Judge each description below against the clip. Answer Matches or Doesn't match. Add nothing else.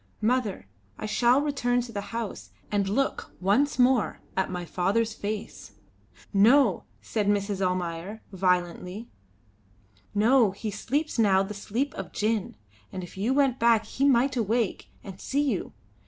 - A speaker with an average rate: Matches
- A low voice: Doesn't match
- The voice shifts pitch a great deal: Doesn't match